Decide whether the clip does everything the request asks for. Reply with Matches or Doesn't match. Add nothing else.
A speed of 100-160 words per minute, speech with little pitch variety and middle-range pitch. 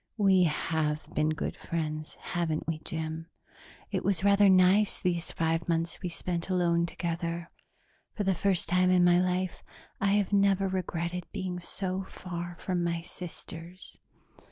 Matches